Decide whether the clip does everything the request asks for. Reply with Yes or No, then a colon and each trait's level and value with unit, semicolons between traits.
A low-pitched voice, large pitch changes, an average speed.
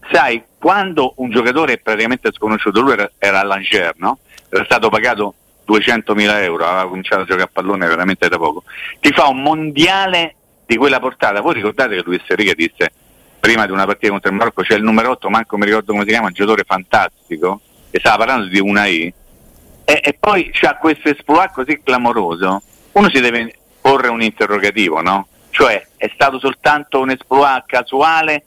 No: low, 120 Hz; wide, 6.0 semitones; fast, 185 wpm